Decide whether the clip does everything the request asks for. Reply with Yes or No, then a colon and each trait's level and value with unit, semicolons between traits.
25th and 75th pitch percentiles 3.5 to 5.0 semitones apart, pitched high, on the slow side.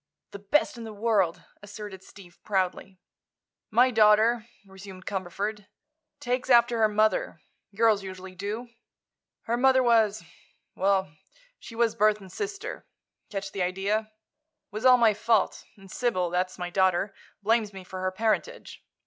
No: average, 3.1 semitones; high, 210 Hz; slow, 130 wpm